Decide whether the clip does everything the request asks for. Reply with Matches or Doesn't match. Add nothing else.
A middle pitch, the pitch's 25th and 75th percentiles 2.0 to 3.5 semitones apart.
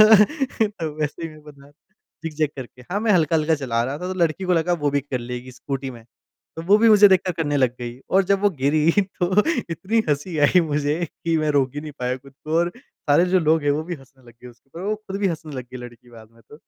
Doesn't match